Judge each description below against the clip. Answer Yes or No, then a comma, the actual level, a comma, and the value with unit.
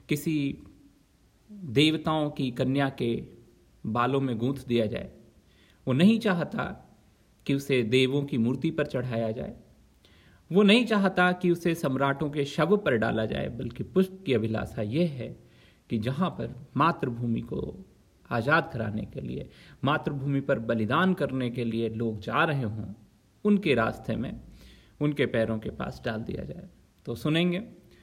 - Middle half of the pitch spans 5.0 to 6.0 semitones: Yes, wide, 5.6 semitones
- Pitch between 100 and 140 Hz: Yes, low, 135 Hz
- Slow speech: No, average, 150 wpm